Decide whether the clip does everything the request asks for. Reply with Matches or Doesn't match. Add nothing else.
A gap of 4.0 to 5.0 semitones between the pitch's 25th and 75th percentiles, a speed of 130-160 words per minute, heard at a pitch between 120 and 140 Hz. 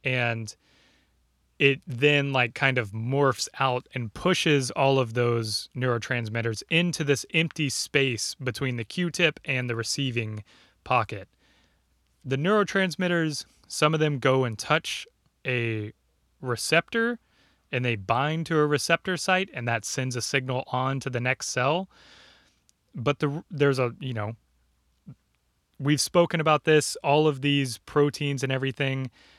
Matches